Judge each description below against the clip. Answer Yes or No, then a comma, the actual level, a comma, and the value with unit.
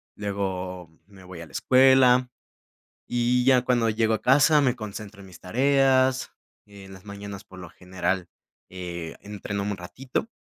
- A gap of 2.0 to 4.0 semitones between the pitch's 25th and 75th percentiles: No, average, 5.2 semitones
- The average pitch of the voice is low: Yes, low, 105 Hz